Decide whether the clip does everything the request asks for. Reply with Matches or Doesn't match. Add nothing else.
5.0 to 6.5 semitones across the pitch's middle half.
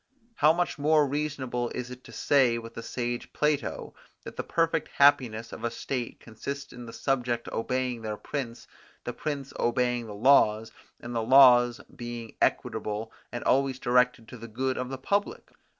Doesn't match